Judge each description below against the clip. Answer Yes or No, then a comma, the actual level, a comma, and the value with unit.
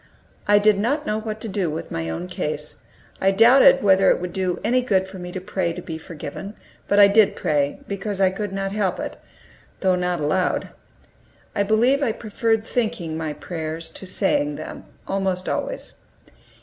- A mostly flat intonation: No, average, 3.2 semitones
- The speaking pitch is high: Yes, high, 195 Hz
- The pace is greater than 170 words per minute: Yes, average, 185 wpm